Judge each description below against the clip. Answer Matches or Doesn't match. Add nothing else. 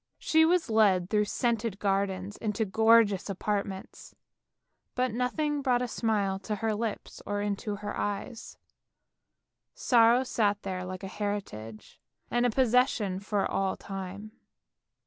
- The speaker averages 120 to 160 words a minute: Matches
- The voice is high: Matches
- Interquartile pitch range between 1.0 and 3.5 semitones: Matches